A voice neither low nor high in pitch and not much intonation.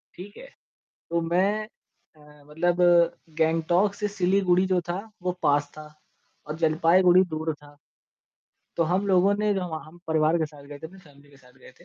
No: medium, 170 Hz; average, 3.3 semitones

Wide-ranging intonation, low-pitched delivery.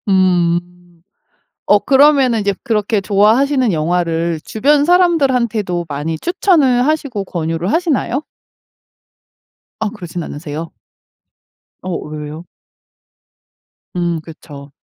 No: wide, 7.7 semitones; high, 195 Hz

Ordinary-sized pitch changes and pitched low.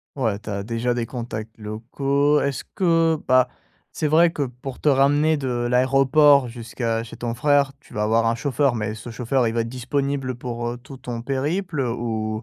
Yes: average, 3.4 semitones; low, 125 Hz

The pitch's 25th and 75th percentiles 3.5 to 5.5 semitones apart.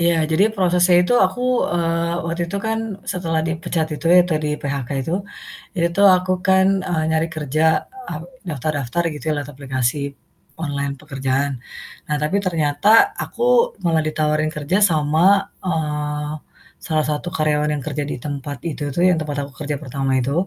No: average, 2.7 semitones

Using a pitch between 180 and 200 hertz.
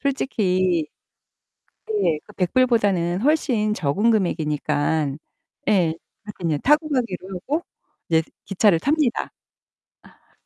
Yes: high, 195 Hz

